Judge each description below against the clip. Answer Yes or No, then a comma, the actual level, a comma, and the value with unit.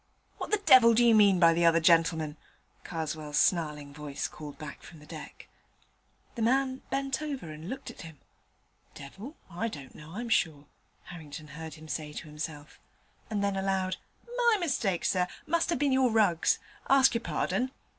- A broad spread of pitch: Yes, wide, 7.8 semitones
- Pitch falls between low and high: Yes, medium, 175 Hz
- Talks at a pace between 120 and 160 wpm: No, average, 180 wpm